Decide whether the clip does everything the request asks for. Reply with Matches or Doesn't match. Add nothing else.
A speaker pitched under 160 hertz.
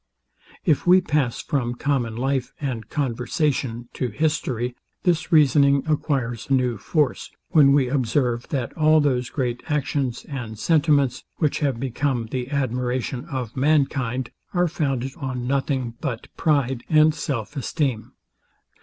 Matches